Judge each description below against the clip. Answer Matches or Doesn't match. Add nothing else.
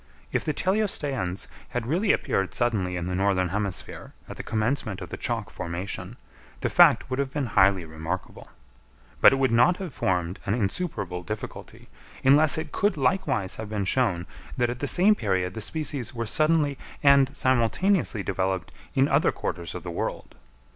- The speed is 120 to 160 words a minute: Doesn't match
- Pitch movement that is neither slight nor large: Doesn't match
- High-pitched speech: Doesn't match